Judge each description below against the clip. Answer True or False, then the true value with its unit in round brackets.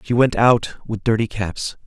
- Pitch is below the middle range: True (110 Hz)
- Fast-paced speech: False (195 wpm)